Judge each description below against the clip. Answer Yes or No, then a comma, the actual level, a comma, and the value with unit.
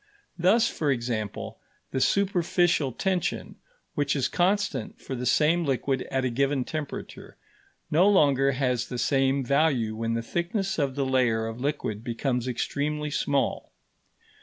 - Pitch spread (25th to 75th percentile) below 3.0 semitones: No, average, 4.4 semitones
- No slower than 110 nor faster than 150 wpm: Yes, average, 140 wpm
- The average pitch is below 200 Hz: Yes, medium, 140 Hz